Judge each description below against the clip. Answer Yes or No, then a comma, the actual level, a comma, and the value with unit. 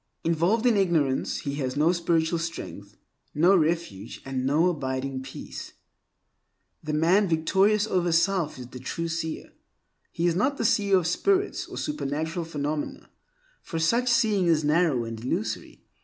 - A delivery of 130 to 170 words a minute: Yes, average, 150 wpm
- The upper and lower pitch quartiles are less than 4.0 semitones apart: No, average, 4.5 semitones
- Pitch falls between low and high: Yes, medium, 165 Hz